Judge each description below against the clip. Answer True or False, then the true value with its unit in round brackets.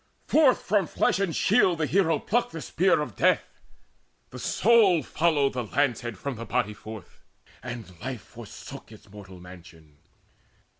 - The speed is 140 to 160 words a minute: True (155 wpm)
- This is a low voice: True (130 Hz)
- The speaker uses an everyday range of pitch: False (8.5 semitones)